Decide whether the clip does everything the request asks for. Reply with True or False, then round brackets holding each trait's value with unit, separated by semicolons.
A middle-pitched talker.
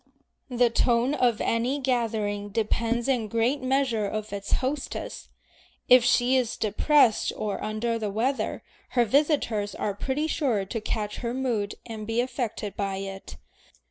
False (230 Hz)